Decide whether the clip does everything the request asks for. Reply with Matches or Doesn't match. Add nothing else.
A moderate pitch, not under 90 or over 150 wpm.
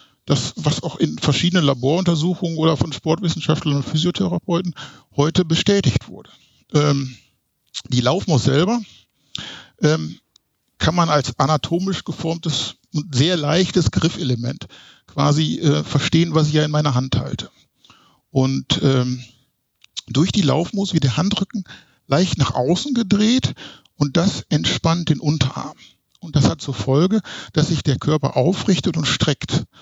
Matches